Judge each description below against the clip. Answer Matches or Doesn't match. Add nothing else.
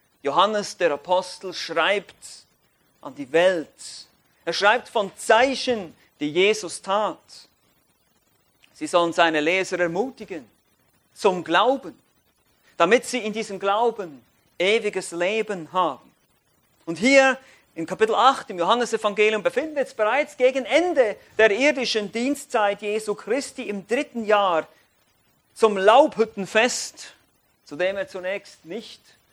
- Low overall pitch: Doesn't match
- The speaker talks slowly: Matches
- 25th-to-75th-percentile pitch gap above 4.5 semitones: Matches